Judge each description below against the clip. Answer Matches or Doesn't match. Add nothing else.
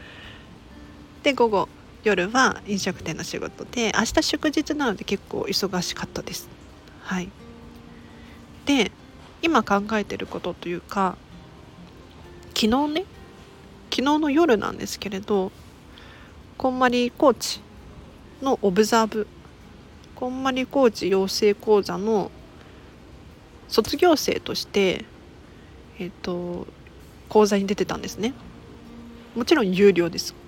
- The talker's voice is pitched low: Doesn't match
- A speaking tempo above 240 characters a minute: Doesn't match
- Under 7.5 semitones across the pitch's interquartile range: Matches